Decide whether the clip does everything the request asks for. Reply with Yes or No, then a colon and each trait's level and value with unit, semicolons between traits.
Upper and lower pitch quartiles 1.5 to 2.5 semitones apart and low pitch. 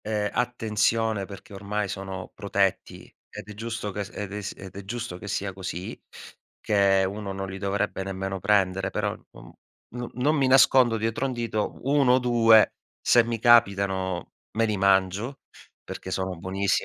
No: average, 2.9 semitones; low, 100 Hz